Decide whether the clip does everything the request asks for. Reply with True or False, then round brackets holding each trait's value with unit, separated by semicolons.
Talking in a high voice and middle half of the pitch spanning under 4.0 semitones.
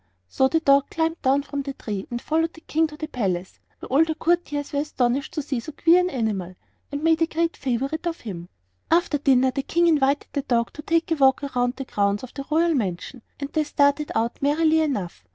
False (285 Hz; 4.3 semitones)